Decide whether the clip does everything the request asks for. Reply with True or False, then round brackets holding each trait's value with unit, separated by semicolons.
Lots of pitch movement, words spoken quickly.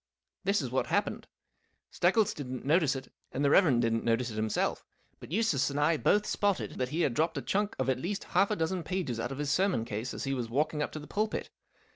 True (6.4 semitones; 235 wpm)